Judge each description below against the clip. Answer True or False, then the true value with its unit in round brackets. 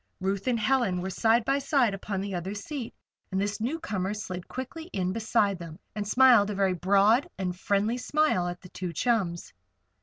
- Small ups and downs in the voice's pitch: False (4.3 semitones)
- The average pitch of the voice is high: True (205 Hz)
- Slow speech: False (185 wpm)